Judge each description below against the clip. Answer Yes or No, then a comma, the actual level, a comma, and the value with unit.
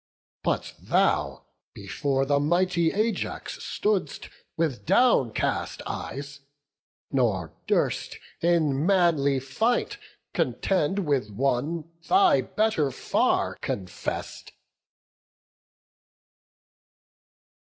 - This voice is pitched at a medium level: Yes, medium, 150 Hz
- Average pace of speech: No, slow, 75 wpm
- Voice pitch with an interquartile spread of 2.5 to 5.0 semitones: No, wide, 5.6 semitones